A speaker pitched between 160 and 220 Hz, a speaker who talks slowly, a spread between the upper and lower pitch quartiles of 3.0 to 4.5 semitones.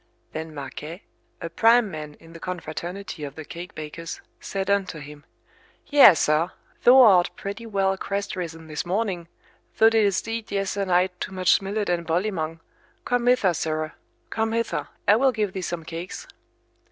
No: medium, 185 Hz; average, 160 wpm; average, 4.1 semitones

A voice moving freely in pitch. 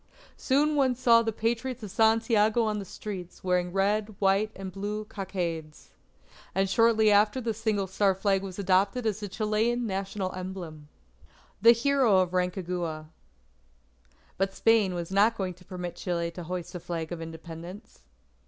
No: average, 3.4 semitones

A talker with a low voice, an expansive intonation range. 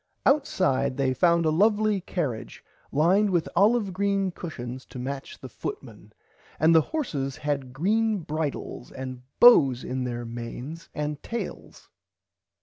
No: medium, 155 Hz; wide, 7.0 semitones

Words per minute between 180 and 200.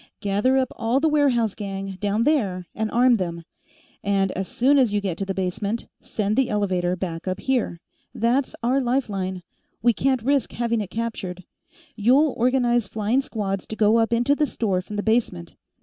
Yes: average, 185 wpm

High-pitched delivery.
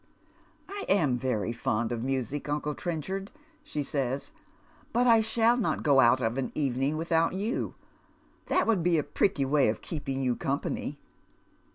No: medium, 145 Hz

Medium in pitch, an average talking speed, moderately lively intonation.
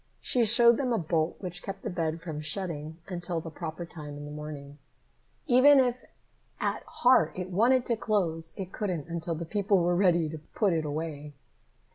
Yes: medium, 175 Hz; average, 185 wpm; average, 4.5 semitones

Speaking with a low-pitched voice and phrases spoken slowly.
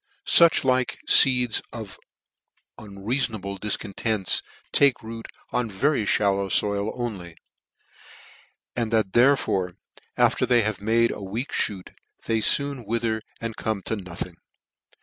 Yes: low, 110 Hz; slow, 120 wpm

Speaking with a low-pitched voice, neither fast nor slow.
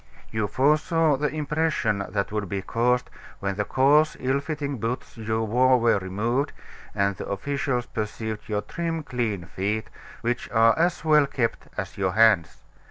Yes: low, 120 Hz; average, 160 wpm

